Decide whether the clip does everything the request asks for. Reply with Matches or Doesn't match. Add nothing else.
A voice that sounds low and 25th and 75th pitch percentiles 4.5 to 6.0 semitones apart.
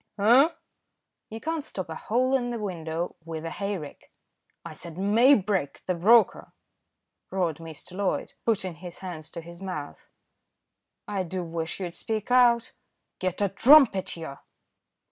Doesn't match